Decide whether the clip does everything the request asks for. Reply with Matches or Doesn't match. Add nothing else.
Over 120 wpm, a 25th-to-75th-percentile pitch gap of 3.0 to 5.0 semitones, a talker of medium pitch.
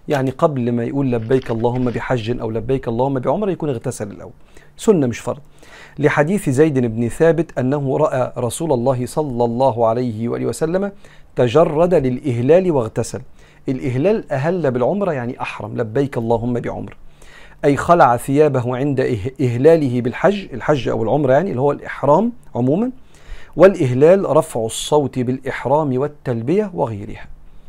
Doesn't match